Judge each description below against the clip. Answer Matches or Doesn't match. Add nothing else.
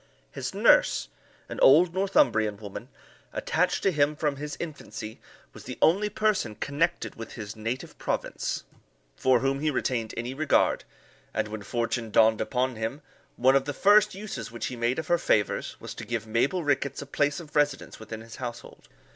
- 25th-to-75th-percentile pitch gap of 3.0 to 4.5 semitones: Doesn't match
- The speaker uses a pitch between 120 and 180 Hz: Matches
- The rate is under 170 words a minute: Doesn't match